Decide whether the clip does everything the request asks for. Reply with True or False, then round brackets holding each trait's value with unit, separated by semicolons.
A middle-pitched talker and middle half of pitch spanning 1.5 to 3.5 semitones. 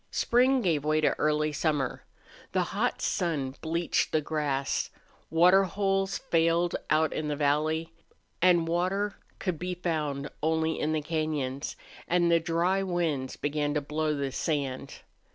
True (160 Hz; 2.7 semitones)